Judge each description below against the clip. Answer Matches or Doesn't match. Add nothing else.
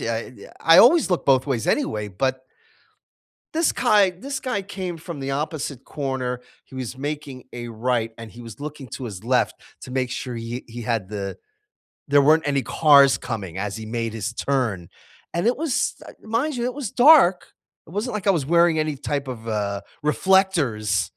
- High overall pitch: Doesn't match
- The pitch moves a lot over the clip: Matches